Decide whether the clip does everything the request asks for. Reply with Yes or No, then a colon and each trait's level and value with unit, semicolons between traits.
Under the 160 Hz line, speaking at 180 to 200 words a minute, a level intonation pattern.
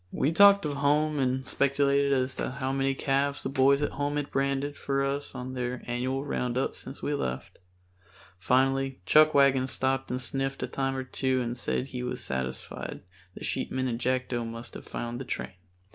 Yes: low, 135 Hz; average, 185 wpm; narrow, 1.6 semitones